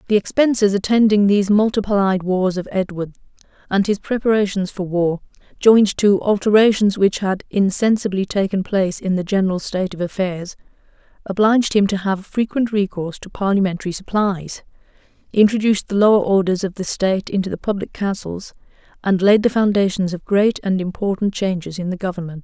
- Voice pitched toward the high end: Yes, high, 195 Hz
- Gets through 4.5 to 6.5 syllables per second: Yes, 5.6 syllables/s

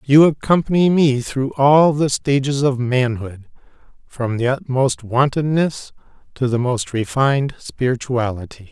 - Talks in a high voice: No, low, 135 Hz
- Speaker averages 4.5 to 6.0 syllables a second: No, 4.2 syllables/s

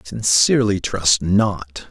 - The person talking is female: No, male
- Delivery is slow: Yes, slow, 125 wpm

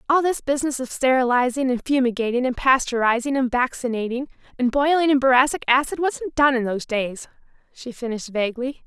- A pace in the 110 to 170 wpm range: Yes, average, 160 wpm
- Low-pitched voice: No, very high, 255 Hz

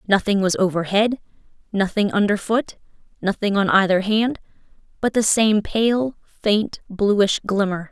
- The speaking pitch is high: Yes, high, 205 Hz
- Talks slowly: Yes, slow, 130 wpm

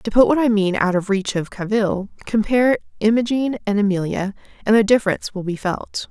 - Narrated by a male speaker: No, female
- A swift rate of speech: No, average, 195 wpm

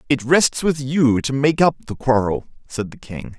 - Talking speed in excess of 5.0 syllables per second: No, 4.5 syllables/s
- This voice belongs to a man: Yes, male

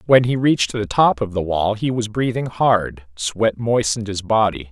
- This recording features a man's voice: Yes, male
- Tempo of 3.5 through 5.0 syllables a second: Yes, 4.7 syllables/s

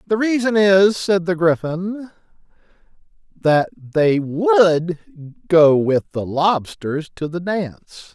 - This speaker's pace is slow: Yes, slow, 120 wpm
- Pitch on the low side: No, medium, 175 Hz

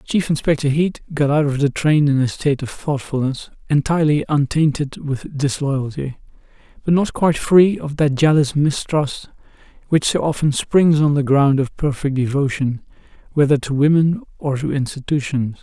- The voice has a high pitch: No, medium, 145 Hz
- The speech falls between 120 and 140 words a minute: No, average, 155 wpm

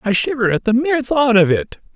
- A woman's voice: No, male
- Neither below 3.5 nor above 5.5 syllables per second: No, 5.8 syllables/s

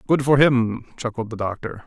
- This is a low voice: Yes, low, 125 Hz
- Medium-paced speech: Yes, average, 195 wpm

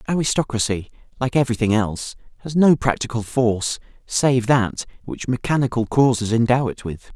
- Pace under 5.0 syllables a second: No, 5.4 syllables/s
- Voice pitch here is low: Yes, low, 120 Hz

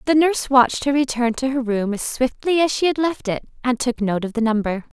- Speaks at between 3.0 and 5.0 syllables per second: No, 5.8 syllables/s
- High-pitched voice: Yes, very high, 255 Hz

